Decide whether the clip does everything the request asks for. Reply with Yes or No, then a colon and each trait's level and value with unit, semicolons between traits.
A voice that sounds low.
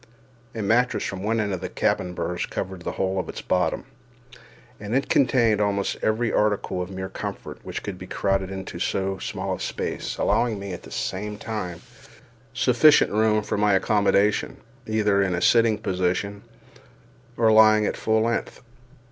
Yes: low, 105 Hz